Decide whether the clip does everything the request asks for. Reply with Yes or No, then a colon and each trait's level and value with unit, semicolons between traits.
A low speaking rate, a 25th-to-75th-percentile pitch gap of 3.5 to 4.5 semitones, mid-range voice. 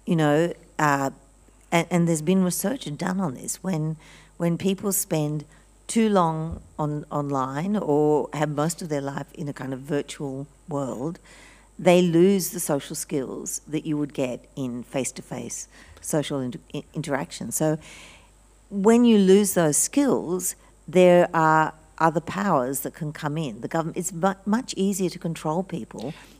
No: average, 150 wpm; average, 3.8 semitones; medium, 160 Hz